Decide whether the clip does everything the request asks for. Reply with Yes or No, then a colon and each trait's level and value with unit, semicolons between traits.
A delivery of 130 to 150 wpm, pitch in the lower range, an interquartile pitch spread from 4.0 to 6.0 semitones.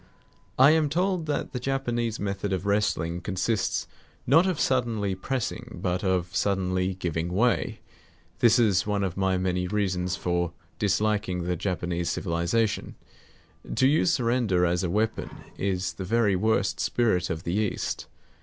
Yes: average, 145 wpm; low, 100 Hz; average, 4.4 semitones